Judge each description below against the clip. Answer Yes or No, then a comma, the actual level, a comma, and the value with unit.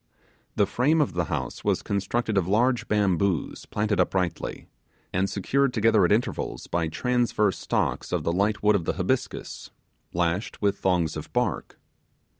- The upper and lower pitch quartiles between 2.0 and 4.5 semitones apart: Yes, average, 4.1 semitones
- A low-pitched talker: Yes, low, 100 Hz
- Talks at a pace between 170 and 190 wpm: No, average, 155 wpm